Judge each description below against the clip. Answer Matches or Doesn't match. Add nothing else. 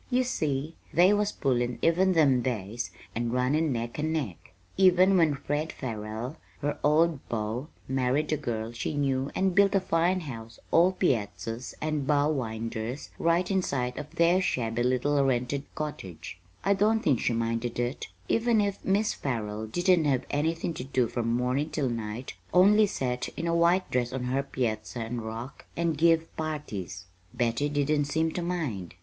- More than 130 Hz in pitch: Matches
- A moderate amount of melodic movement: Doesn't match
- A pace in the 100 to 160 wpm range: Doesn't match